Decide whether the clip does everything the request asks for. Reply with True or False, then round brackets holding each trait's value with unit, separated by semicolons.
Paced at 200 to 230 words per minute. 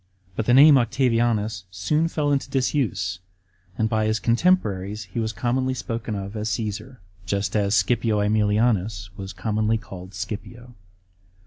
False (140 wpm)